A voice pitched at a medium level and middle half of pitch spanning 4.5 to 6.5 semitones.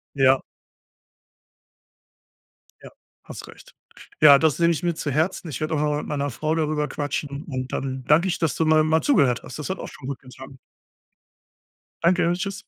No: medium, 150 Hz; average, 2.9 semitones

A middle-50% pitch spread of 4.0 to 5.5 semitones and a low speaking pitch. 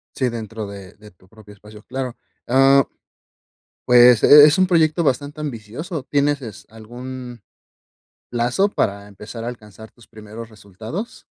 Yes: average, 4.5 semitones; low, 120 Hz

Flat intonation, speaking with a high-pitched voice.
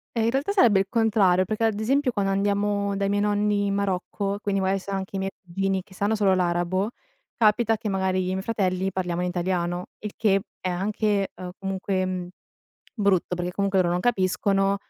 Yes: narrow, 1.8 semitones; high, 195 Hz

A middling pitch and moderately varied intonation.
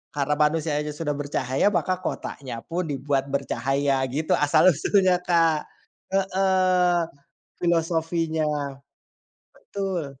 Yes: medium, 160 Hz; average, 3.9 semitones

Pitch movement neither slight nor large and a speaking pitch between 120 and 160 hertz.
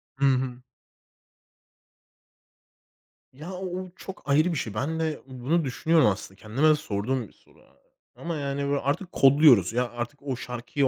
Yes: average, 4.1 semitones; medium, 140 Hz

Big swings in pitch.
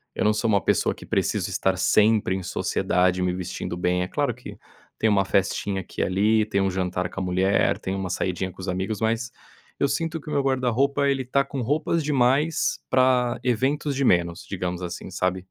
Yes: wide, 5.9 semitones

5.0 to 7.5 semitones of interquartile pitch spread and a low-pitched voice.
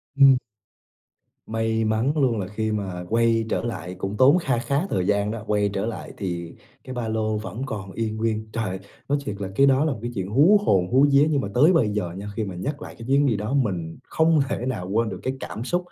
No: average, 4.5 semitones; low, 110 Hz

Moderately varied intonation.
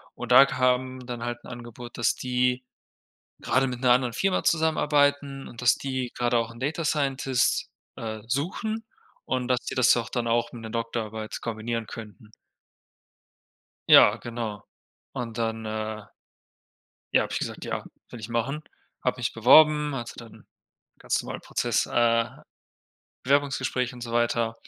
No: narrow, 2.3 semitones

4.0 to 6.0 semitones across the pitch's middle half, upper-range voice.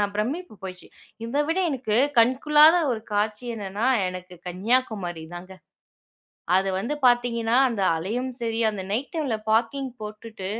Yes: average, 4.6 semitones; high, 225 Hz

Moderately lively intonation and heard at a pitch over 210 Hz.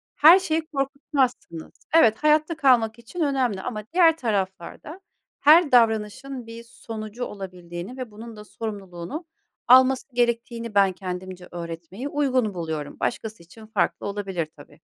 No: wide, 6.0 semitones; high, 225 Hz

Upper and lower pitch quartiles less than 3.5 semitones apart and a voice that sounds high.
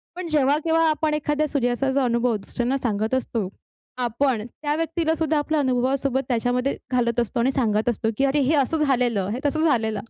No: average, 3.8 semitones; very high, 265 Hz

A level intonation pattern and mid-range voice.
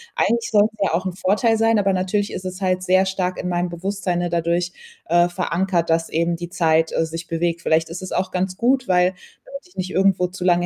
Yes: narrow, 1.8 semitones; medium, 180 Hz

